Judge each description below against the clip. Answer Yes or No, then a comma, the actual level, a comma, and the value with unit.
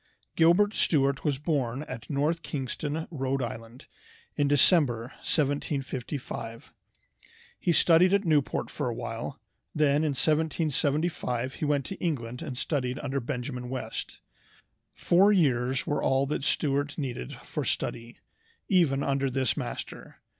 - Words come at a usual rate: No, slow, 125 wpm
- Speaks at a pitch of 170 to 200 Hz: No, medium, 140 Hz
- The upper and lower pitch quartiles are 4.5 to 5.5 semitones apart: No, average, 3.4 semitones